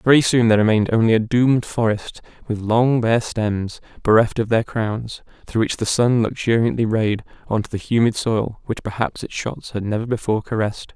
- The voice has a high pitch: No, low, 110 Hz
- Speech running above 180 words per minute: Yes, average, 190 wpm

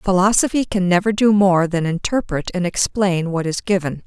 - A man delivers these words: No, female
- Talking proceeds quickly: No, average, 175 wpm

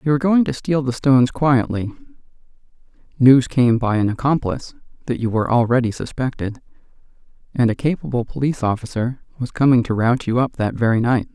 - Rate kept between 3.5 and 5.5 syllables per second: No, 6.0 syllables/s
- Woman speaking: No, male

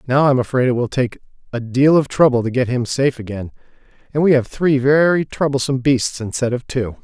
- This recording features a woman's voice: No, male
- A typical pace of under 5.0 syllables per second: No, 5.8 syllables/s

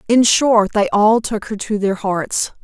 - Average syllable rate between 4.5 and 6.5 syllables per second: No, 4.0 syllables/s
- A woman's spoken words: Yes, female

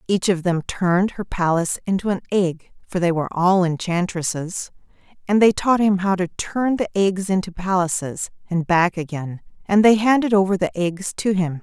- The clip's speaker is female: Yes, female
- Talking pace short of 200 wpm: Yes, average, 175 wpm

